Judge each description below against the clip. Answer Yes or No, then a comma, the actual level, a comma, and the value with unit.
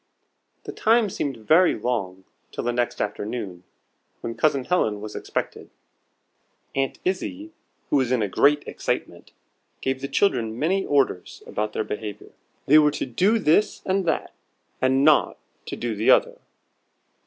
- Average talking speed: Yes, average, 150 wpm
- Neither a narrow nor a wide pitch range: No, wide, 6.7 semitones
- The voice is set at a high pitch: No, low, 130 Hz